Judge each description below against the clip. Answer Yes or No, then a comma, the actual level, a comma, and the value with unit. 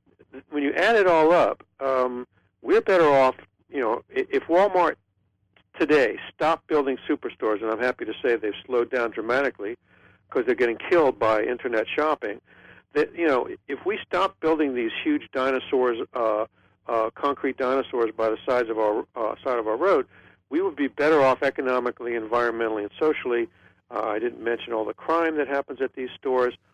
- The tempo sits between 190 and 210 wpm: No, average, 175 wpm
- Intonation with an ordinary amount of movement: No, wide, 7.5 semitones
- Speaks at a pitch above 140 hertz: No, low, 135 Hz